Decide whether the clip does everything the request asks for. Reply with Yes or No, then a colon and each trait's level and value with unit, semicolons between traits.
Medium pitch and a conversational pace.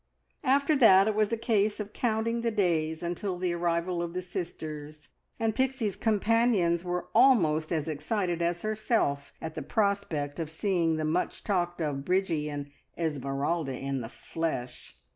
Yes: medium, 175 Hz; average, 160 wpm